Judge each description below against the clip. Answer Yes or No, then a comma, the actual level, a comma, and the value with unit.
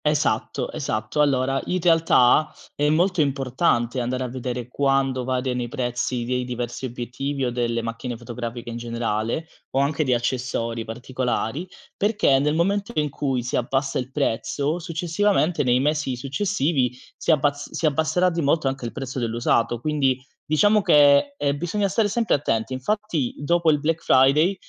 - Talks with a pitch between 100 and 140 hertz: Yes, low, 135 Hz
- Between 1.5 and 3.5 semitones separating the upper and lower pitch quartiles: No, average, 4.1 semitones